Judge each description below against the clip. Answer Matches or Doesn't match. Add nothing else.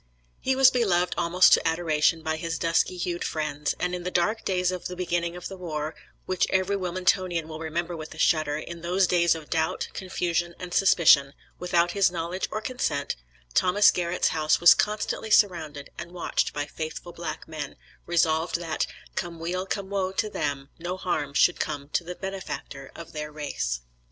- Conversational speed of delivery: Matches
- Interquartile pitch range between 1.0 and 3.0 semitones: Matches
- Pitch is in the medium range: Matches